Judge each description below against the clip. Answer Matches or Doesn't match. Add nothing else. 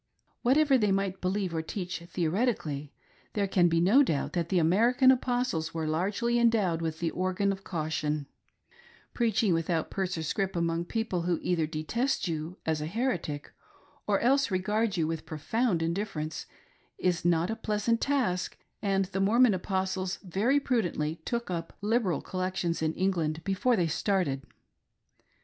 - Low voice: Doesn't match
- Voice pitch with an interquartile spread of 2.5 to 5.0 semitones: Matches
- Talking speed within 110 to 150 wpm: Doesn't match